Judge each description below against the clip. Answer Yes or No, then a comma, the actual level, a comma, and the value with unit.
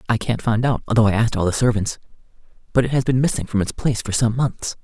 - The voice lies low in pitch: Yes, low, 115 Hz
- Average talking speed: No, fast, 260 wpm